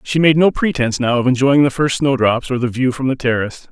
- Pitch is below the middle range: Yes, low, 130 Hz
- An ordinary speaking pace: No, fast, 260 wpm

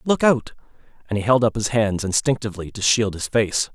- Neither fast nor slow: No, fast, 210 wpm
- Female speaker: No, male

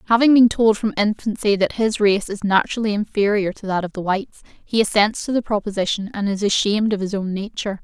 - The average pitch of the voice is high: Yes, high, 210 Hz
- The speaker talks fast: Yes, fast, 215 wpm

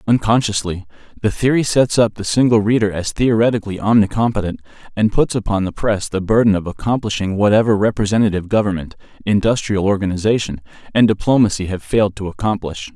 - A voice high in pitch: No, low, 105 Hz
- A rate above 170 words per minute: No, average, 145 wpm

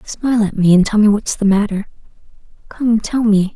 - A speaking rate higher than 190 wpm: Yes, fast, 205 wpm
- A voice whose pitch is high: Yes, high, 210 Hz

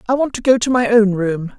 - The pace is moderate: No, fast, 305 wpm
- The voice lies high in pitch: Yes, high, 225 Hz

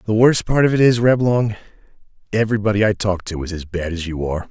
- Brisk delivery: Yes, fast, 225 wpm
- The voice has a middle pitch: No, low, 105 Hz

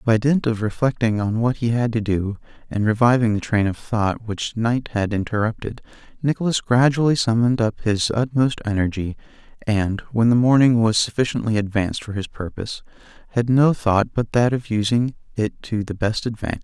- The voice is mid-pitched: No, low, 115 Hz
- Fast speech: No, average, 175 wpm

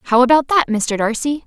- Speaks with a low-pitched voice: No, very high, 255 Hz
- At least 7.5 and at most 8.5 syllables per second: No, 4.9 syllables/s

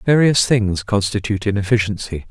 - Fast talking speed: No, slow, 105 wpm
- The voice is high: No, low, 105 Hz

